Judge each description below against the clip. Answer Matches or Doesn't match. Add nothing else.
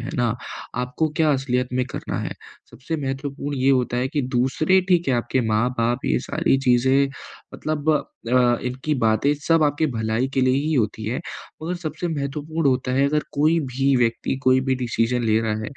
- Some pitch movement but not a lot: Matches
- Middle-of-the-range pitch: Doesn't match